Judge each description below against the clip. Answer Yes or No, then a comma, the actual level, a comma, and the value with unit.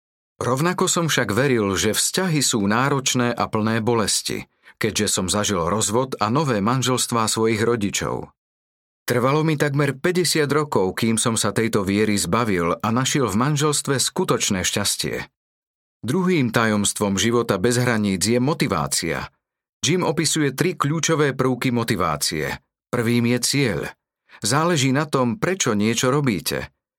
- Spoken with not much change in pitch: No, wide, 5.5 semitones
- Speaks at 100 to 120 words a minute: No, average, 130 wpm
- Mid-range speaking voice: No, low, 120 Hz